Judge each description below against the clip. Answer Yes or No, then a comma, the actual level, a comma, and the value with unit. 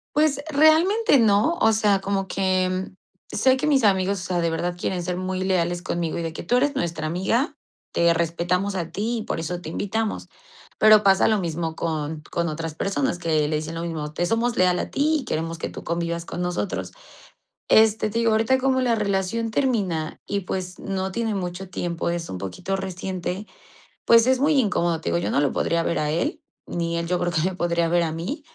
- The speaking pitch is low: No, medium, 185 Hz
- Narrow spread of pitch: No, average, 4.6 semitones